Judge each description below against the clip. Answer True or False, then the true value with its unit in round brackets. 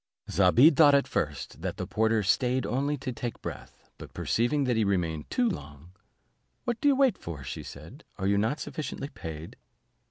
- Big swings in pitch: True (7.8 semitones)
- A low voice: True (115 Hz)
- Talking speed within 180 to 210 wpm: True (185 wpm)